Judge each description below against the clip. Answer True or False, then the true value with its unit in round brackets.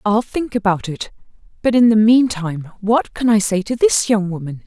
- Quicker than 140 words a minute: True (205 wpm)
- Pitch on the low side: False (215 Hz)